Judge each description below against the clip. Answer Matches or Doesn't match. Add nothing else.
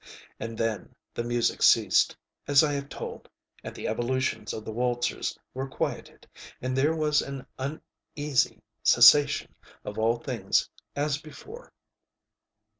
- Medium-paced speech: Doesn't match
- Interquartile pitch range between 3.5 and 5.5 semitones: Matches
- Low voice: Matches